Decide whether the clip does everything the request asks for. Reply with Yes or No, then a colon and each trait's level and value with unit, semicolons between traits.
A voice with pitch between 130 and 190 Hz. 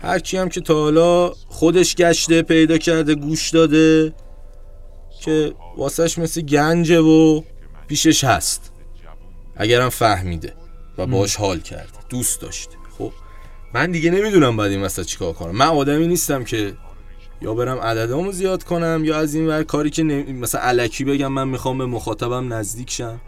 Yes: low, 135 Hz